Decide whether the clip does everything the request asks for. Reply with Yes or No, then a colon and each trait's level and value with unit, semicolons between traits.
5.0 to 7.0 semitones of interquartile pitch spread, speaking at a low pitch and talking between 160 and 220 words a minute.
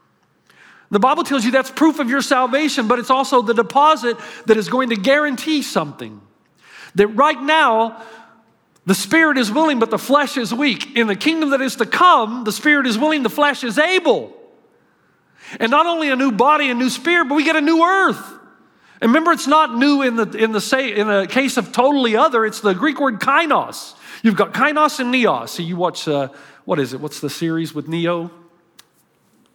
No: wide, 5.5 semitones; very high, 255 Hz; fast, 205 wpm